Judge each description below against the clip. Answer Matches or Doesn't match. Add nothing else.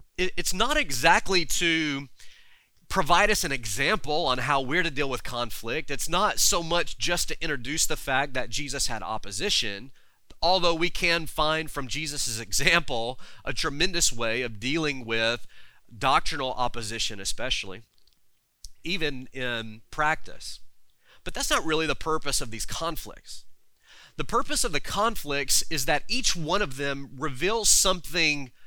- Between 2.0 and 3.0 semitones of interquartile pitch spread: Doesn't match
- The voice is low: Doesn't match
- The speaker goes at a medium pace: Matches